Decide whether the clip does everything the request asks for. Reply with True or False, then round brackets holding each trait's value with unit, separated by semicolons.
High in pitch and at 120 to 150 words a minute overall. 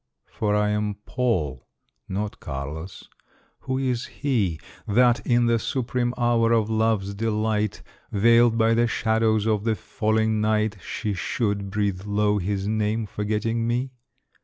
False (110 Hz; 135 wpm)